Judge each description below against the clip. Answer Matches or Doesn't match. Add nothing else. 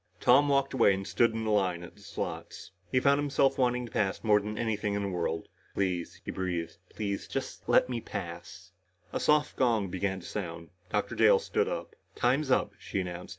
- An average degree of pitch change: Doesn't match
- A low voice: Matches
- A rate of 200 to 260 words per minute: Matches